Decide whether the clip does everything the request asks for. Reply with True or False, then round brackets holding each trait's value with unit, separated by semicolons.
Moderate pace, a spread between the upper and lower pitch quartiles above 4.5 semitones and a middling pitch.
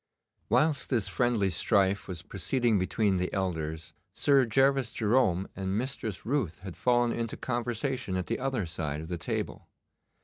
False (150 wpm; 5.1 semitones; 110 Hz)